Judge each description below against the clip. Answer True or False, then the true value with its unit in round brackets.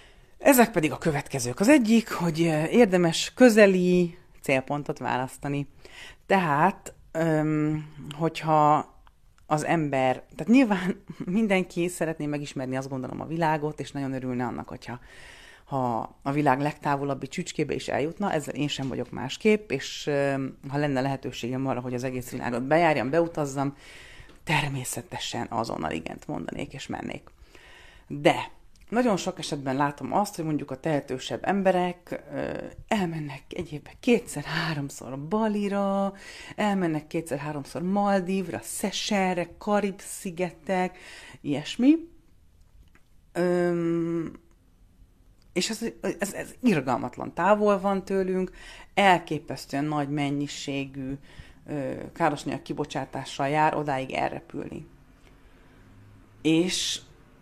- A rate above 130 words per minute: False (105 wpm)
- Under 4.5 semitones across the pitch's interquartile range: False (5.2 semitones)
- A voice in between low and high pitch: True (155 Hz)